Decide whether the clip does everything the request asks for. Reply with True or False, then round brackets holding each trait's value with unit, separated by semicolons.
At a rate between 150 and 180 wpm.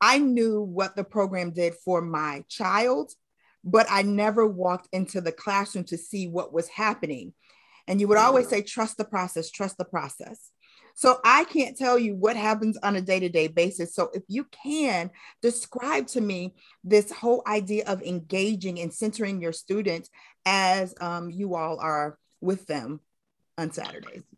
True (170 wpm)